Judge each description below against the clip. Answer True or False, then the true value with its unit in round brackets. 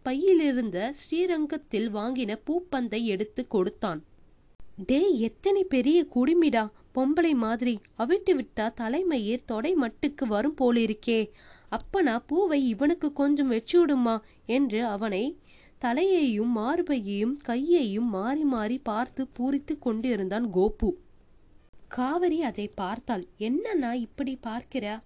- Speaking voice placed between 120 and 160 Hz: False (245 Hz)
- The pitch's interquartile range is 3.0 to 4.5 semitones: False (5.2 semitones)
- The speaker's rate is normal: True (100 wpm)